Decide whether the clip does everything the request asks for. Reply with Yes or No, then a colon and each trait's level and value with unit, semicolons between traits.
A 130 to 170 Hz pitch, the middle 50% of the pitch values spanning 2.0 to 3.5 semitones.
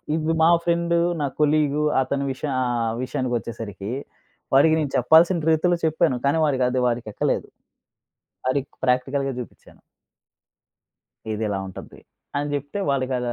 No: medium, 140 Hz; average, 4.0 semitones